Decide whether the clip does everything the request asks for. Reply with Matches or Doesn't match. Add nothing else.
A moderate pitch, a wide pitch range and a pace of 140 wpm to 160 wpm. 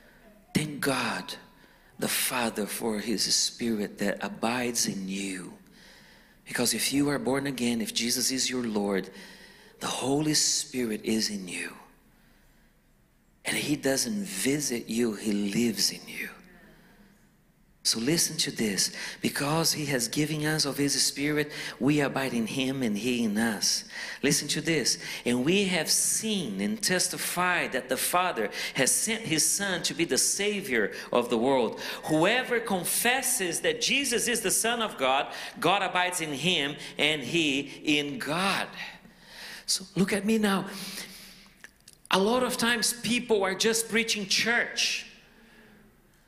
Matches